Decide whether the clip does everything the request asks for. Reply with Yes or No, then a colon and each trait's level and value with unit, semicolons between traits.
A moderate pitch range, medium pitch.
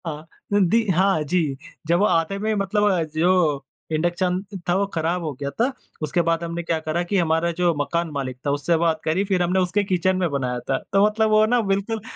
Yes: average, 3.6 semitones; medium, 175 Hz